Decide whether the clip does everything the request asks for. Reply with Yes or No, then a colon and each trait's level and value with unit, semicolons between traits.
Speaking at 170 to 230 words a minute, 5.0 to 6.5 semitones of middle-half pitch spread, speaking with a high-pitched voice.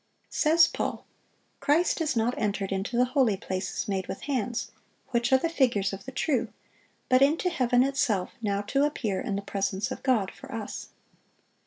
Yes: average, 175 wpm; wide, 5.5 semitones; high, 240 Hz